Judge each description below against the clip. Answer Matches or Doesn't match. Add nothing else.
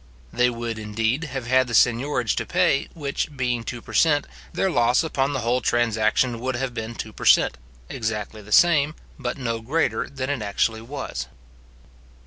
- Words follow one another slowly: Doesn't match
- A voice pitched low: Matches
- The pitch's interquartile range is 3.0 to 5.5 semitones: Matches